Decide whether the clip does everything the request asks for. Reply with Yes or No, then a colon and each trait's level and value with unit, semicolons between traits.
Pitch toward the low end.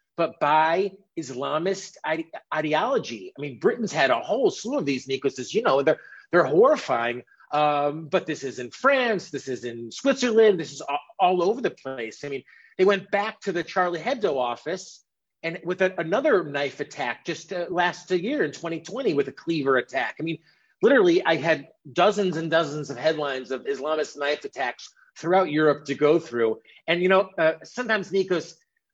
No: medium, 160 Hz